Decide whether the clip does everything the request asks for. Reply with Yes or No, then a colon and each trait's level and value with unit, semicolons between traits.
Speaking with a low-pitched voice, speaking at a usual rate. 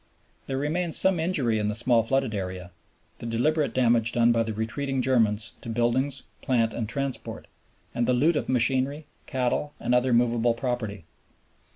Yes: low, 120 Hz; average, 165 wpm